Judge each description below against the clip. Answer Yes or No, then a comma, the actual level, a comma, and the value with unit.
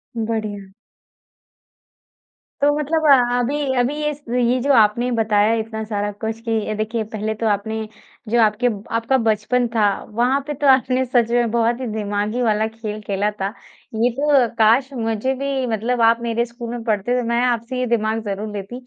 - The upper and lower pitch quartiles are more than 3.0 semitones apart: No, narrow, 2.4 semitones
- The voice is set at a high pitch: Yes, high, 230 Hz